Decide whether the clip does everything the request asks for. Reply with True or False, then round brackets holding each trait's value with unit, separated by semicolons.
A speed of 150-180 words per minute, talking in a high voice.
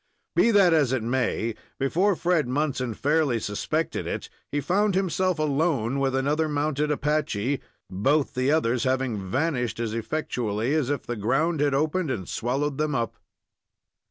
False (155 wpm; 140 Hz)